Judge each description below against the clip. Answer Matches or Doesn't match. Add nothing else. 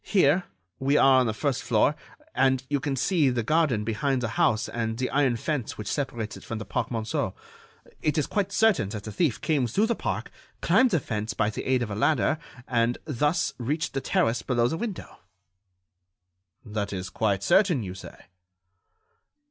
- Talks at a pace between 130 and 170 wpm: Doesn't match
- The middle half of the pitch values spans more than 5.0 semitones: Matches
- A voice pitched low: Matches